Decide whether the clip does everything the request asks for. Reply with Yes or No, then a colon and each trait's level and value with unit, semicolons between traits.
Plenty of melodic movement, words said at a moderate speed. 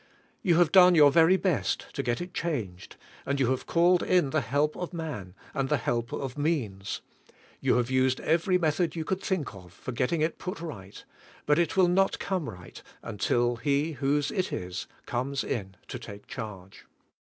Yes: wide, 6.1 semitones; average, 190 wpm